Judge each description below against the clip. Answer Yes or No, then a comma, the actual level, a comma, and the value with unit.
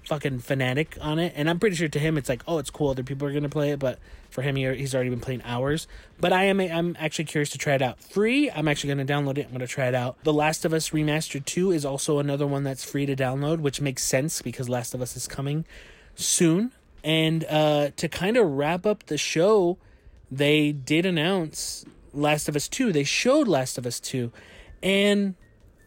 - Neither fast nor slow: No, fast, 225 wpm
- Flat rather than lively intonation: No, average, 3.8 semitones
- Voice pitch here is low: No, medium, 145 Hz